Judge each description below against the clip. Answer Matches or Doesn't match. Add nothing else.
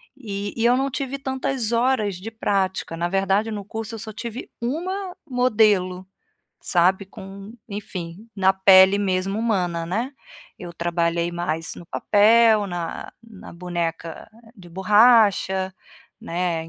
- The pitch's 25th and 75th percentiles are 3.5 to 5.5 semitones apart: Matches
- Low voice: Doesn't match